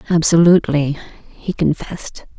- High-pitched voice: No, medium, 160 Hz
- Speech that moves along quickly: No, slow, 75 wpm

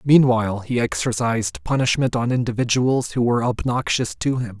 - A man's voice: Yes, male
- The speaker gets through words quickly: No, average, 145 wpm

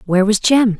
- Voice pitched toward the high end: Yes, high, 210 Hz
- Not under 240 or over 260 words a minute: No, fast, 225 wpm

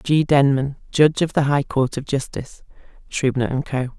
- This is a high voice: No, medium, 140 Hz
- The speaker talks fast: No, average, 180 wpm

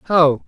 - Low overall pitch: No, medium, 160 Hz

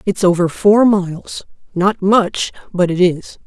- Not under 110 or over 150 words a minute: Yes, average, 140 wpm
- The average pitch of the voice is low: No, high, 190 Hz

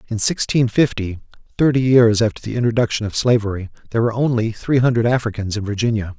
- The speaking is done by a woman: No, male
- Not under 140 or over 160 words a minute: No, average, 175 wpm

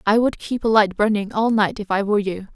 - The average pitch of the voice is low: No, high, 210 Hz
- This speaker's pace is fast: Yes, fast, 280 wpm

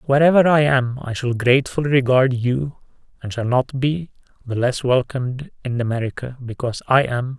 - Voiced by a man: Yes, male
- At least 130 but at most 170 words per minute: Yes, average, 165 wpm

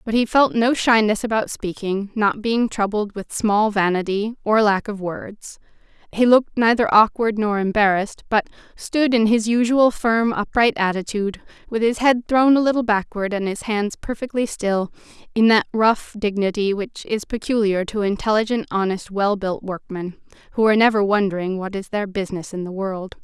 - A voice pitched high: Yes, high, 210 Hz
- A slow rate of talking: No, average, 175 wpm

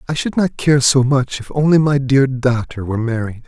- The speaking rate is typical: No, fast, 225 wpm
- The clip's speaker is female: No, male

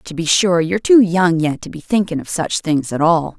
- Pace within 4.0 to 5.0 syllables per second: No, 5.2 syllables/s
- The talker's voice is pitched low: No, medium, 170 Hz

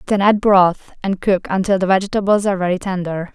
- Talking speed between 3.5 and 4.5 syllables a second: No, 5.9 syllables/s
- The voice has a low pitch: No, high, 190 Hz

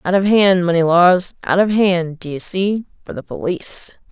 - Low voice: No, medium, 180 Hz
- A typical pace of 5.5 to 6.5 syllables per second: No, 4.4 syllables/s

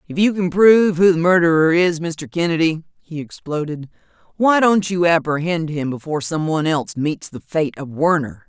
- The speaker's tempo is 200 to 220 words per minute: No, average, 185 wpm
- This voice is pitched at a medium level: Yes, medium, 165 Hz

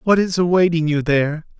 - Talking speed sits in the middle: Yes, average, 190 wpm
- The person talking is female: No, male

